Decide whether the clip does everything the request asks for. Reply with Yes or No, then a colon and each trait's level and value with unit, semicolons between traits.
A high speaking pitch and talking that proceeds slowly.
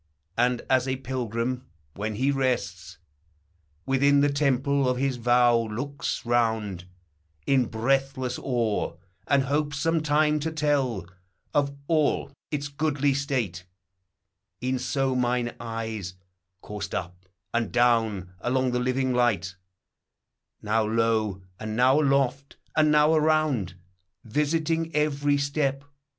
No: low, 130 Hz; slow, 120 wpm